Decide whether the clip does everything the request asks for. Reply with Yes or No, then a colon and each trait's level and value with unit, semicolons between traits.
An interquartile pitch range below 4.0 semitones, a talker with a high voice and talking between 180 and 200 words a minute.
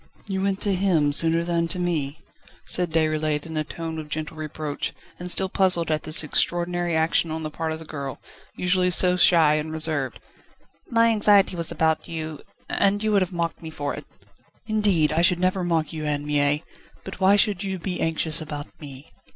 No: average, 2.8 semitones; medium, 165 Hz; average, 195 wpm